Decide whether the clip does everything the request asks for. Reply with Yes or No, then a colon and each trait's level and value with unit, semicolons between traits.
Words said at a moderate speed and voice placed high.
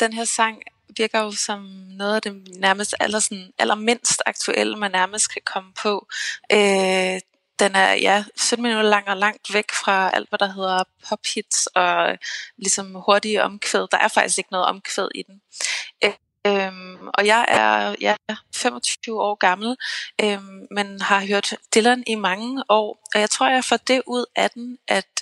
Yes: average, 175 wpm; high, 205 Hz